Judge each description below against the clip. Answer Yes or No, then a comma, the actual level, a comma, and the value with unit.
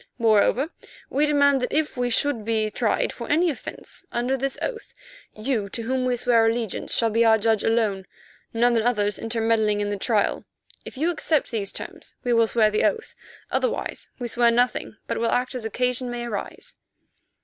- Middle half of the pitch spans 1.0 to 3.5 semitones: Yes, narrow, 2.6 semitones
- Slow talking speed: No, average, 180 wpm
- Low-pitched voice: No, high, 235 Hz